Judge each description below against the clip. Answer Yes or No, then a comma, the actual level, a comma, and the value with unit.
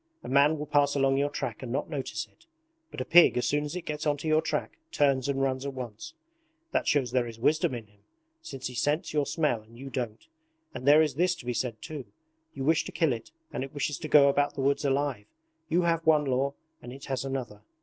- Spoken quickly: Yes, fast, 240 wpm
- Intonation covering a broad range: No, average, 2.8 semitones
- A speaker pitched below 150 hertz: Yes, medium, 140 Hz